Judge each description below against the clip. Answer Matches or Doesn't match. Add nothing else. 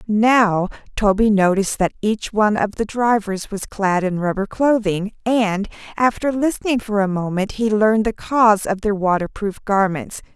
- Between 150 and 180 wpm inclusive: Matches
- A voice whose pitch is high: Matches